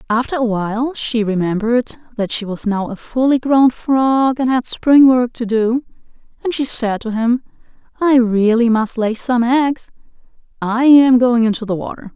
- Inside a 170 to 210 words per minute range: Yes, average, 180 wpm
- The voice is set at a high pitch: Yes, high, 240 Hz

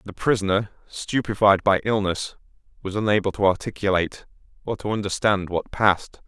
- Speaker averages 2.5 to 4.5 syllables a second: No, 5.5 syllables/s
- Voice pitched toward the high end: No, low, 100 Hz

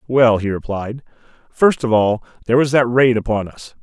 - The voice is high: No, low, 120 Hz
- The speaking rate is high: No, average, 190 wpm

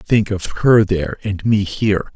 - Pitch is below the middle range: Yes, low, 100 Hz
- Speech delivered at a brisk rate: No, average, 195 wpm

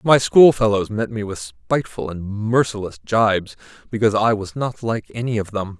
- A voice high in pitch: No, low, 105 Hz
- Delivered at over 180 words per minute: No, average, 175 wpm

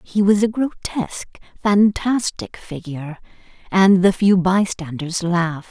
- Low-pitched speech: No, high, 190 Hz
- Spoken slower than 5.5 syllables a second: Yes, 4.2 syllables/s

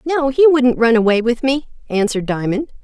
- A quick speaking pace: No, average, 190 wpm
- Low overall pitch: No, very high, 250 Hz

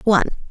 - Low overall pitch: No, high, 205 Hz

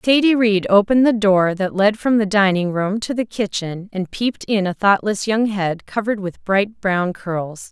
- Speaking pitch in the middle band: No, high, 200 Hz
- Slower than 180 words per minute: No, average, 200 wpm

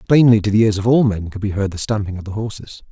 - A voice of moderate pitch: No, low, 105 Hz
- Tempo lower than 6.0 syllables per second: No, 6.7 syllables/s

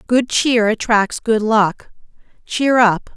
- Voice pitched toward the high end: Yes, high, 225 Hz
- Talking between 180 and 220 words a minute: No, slow, 135 wpm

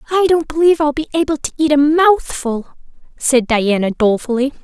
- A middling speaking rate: Yes, average, 170 wpm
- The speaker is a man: No, female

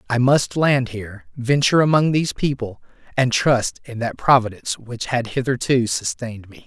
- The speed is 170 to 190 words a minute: No, average, 160 wpm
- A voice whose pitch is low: Yes, low, 120 Hz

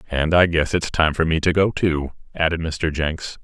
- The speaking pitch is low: Yes, very low, 80 Hz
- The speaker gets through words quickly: Yes, fast, 225 wpm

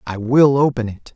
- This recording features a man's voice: Yes, male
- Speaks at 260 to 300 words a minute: No, fast, 210 wpm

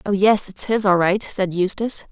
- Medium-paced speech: No, fast, 225 wpm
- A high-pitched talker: Yes, high, 200 Hz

